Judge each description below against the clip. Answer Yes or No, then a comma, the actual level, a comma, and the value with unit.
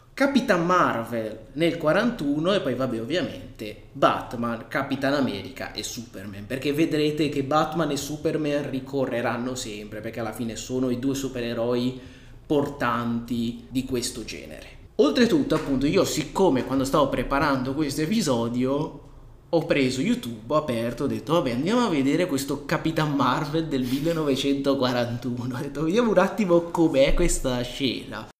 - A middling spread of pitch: Yes, average, 4.2 semitones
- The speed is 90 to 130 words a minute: No, average, 140 wpm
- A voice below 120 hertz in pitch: No, low, 135 Hz